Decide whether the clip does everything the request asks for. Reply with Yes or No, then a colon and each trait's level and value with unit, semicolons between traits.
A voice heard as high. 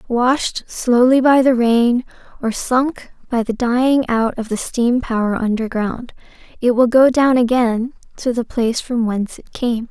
Yes: high, 240 Hz